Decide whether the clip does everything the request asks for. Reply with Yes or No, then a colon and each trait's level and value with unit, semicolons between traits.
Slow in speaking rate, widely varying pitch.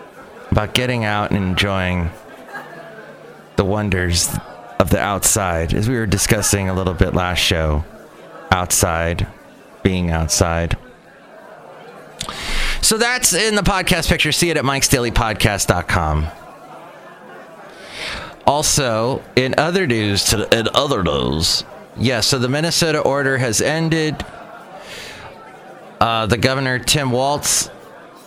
Yes: slow, 120 wpm; wide, 6.5 semitones